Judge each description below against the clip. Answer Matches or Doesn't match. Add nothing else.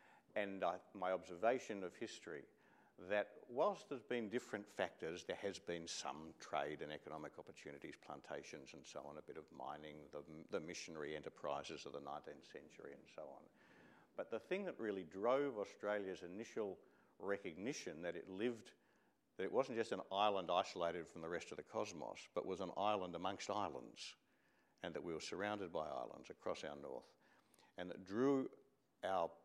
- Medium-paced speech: Matches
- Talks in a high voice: Doesn't match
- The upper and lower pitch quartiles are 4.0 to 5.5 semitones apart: Matches